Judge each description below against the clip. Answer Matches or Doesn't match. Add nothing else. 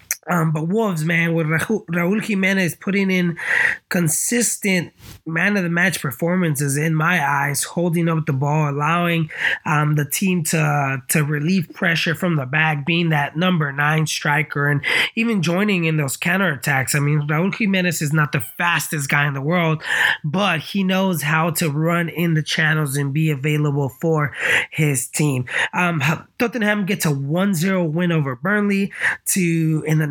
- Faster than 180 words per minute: Doesn't match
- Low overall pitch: Doesn't match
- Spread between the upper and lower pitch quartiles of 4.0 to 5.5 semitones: Doesn't match